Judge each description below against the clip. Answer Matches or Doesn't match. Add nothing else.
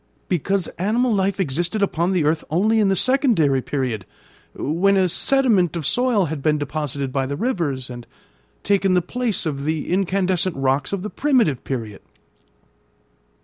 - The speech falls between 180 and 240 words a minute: Doesn't match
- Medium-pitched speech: Matches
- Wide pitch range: Matches